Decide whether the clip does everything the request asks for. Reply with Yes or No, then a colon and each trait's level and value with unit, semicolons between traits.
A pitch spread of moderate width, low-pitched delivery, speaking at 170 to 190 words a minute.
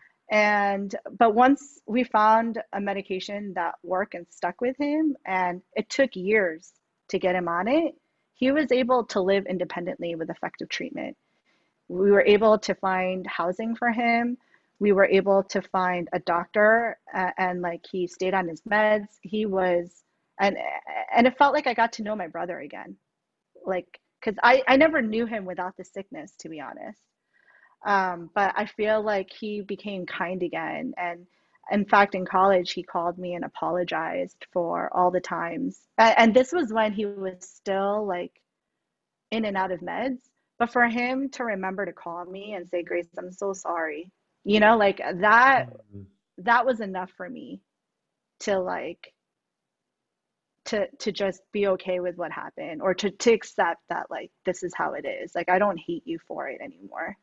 No: average, 4.1 semitones; high, 200 Hz; average, 180 wpm